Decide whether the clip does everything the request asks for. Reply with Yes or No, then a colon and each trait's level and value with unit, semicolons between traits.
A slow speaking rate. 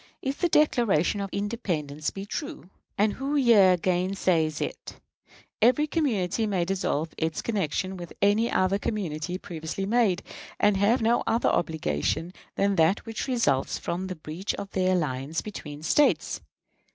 No: average, 145 wpm